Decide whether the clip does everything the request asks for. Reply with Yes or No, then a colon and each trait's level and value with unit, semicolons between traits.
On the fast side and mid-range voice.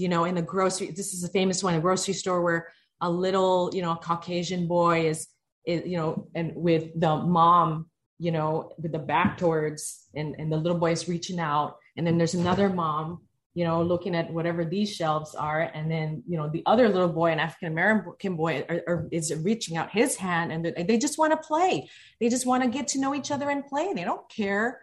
Yes: fast, 225 wpm; medium, 170 Hz